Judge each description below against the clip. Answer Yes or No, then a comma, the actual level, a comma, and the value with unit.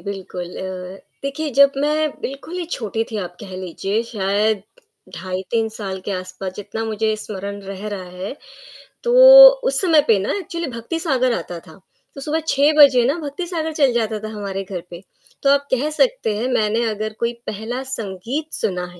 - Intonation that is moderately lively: No, wide, 6.4 semitones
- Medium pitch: No, high, 220 Hz